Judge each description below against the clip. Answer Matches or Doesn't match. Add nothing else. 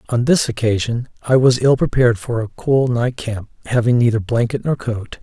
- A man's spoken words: Matches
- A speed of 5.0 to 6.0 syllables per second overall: Matches